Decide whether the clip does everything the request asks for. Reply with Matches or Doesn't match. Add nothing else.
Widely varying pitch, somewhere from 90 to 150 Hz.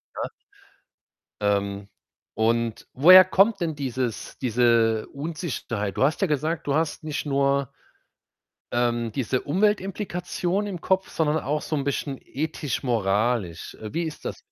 Matches